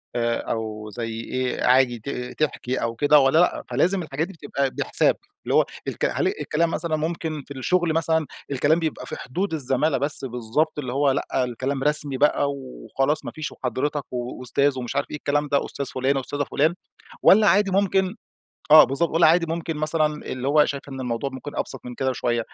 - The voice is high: No, medium, 140 Hz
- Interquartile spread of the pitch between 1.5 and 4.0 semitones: Yes, average, 3.6 semitones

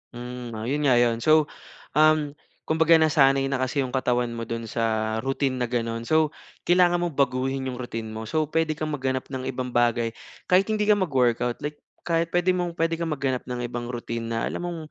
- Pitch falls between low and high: No, low, 130 Hz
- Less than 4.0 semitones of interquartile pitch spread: No, average, 4.6 semitones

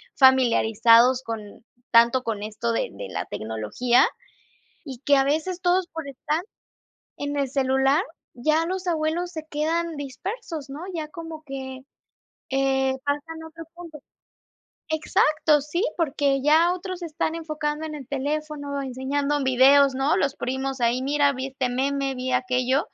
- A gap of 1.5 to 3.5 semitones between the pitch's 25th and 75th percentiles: Yes, average, 3.2 semitones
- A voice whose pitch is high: Yes, very high, 280 Hz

